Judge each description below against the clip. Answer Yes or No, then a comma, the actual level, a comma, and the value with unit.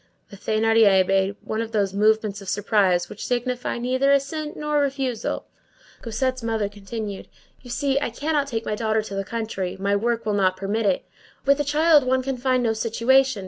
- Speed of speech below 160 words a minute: No, average, 185 wpm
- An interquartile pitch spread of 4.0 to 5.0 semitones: Yes, average, 4.3 semitones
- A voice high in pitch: Yes, high, 225 Hz